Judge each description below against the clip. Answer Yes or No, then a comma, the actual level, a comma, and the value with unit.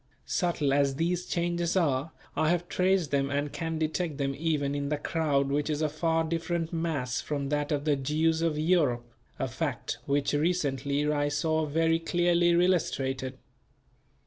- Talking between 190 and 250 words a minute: No, average, 165 wpm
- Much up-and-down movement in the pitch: No, average, 2.8 semitones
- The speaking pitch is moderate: Yes, medium, 155 Hz